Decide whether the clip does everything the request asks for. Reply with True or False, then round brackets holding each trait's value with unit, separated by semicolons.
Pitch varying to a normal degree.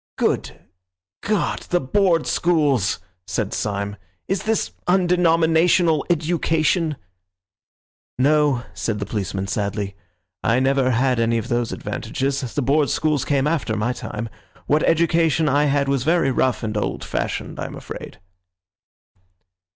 False (5.9 semitones)